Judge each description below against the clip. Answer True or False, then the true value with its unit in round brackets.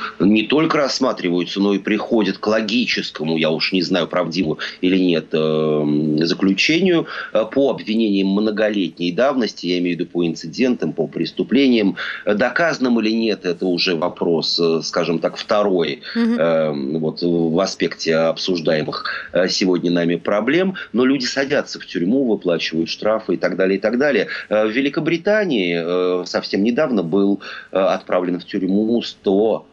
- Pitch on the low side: True (95 Hz)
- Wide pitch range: False (4.5 semitones)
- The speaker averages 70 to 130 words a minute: False (140 wpm)